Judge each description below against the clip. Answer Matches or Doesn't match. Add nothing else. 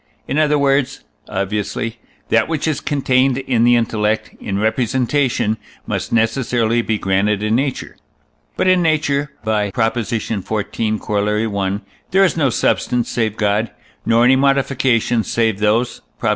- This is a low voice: Matches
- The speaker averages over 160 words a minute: Doesn't match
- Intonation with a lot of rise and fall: Doesn't match